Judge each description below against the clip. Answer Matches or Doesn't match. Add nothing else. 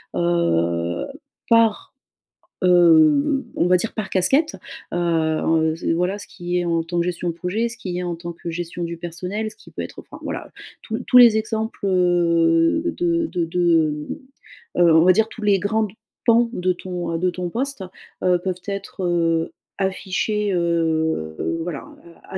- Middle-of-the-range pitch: Matches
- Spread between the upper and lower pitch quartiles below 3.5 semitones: Doesn't match